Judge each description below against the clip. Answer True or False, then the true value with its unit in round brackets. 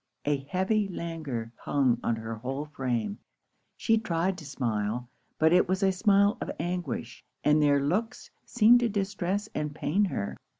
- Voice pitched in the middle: True (165 Hz)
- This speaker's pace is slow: False (160 wpm)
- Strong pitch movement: True (7.1 semitones)